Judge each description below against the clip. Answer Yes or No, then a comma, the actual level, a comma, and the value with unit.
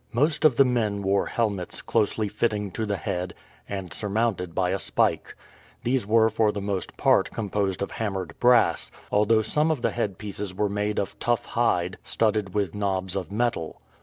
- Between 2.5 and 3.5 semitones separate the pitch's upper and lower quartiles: Yes, average, 2.8 semitones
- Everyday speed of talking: Yes, average, 175 wpm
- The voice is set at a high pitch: No, low, 105 Hz